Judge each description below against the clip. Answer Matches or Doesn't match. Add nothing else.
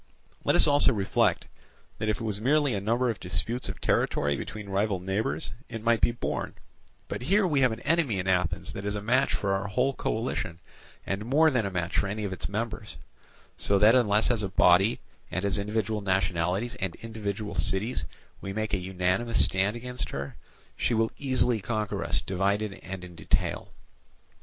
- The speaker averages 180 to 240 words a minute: Matches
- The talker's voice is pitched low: Matches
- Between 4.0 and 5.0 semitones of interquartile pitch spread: Doesn't match